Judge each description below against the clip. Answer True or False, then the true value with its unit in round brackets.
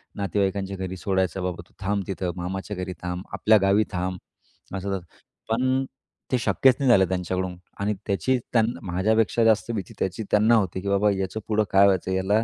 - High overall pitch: False (100 Hz)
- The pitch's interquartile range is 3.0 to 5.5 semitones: False (2.5 semitones)